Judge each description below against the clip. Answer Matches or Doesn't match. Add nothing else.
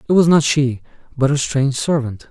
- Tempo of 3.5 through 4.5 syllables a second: Doesn't match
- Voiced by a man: Matches